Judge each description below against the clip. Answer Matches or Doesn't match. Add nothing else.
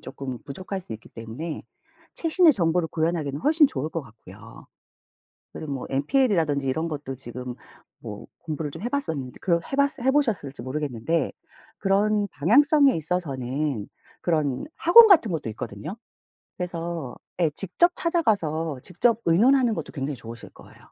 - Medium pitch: Matches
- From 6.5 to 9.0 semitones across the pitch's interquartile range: Matches